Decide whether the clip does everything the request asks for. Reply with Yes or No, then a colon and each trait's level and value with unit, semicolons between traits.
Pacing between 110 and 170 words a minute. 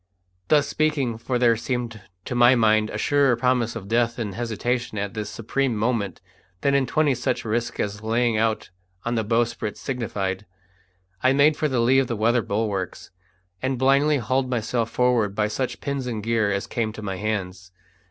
No: average, 180 wpm